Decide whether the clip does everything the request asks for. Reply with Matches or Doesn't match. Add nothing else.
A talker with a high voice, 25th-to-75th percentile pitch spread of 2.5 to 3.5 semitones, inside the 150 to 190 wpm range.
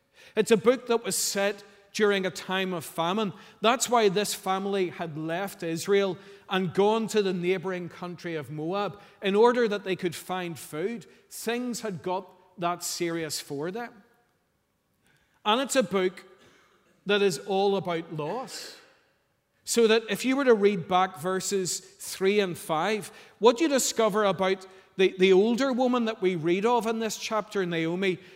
Matches